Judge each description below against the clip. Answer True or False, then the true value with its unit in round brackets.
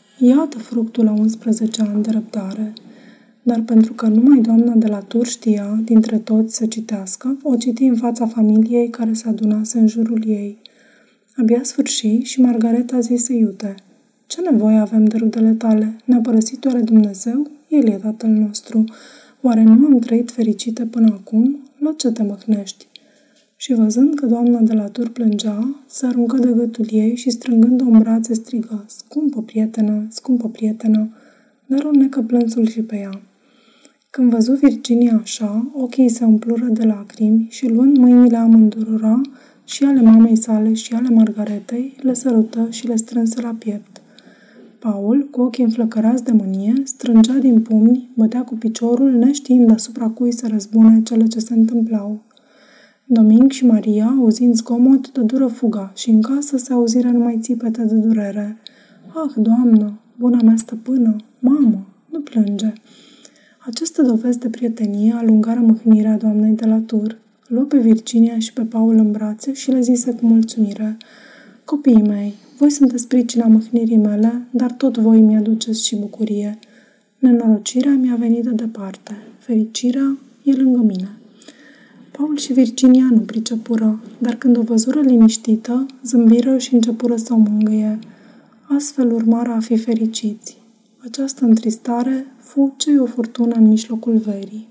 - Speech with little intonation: True (2.2 semitones)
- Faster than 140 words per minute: True (150 wpm)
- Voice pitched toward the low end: False (230 Hz)